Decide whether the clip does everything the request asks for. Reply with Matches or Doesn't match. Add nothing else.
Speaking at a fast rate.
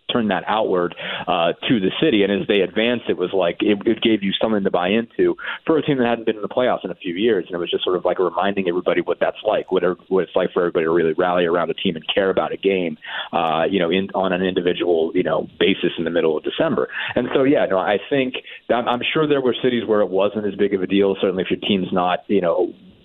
Matches